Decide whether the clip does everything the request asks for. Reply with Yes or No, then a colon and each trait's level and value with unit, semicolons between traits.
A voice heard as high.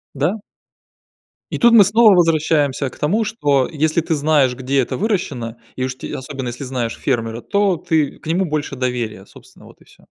No: medium, 145 Hz